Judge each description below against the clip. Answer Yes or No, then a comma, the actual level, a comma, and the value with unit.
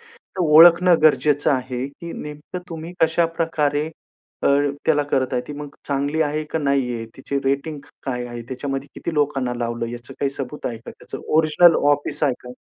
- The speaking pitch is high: No, medium, 145 Hz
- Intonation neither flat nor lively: Yes, average, 3.3 semitones